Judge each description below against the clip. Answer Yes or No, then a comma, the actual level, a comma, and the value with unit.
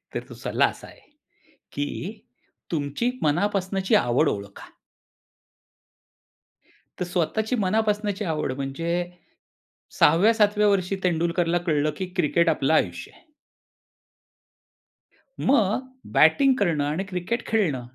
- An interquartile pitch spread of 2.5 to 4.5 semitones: No, average, 5.2 semitones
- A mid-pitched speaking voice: Yes, medium, 175 Hz